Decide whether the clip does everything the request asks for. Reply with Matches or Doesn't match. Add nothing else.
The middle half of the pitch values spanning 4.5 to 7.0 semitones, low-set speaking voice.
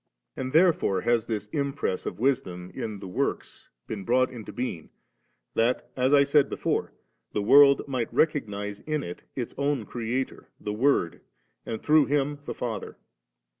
Matches